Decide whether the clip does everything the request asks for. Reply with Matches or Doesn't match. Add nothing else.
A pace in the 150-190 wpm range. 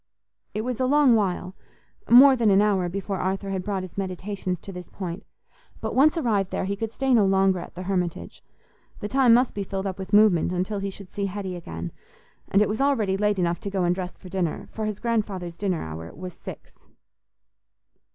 Doesn't match